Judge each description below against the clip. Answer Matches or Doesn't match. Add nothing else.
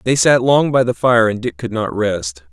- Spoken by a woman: Doesn't match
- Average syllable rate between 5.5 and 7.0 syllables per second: Doesn't match